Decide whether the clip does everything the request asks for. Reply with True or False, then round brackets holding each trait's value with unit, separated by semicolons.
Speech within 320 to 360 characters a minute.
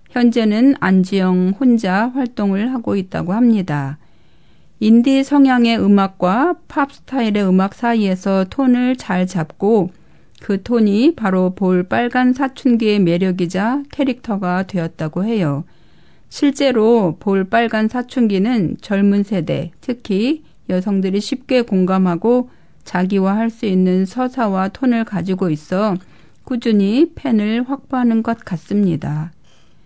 False (255 characters per minute)